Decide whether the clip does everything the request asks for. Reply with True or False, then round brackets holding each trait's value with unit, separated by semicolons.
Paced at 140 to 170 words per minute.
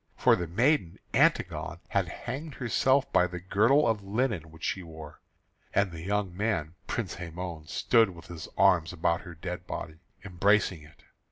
True (165 wpm)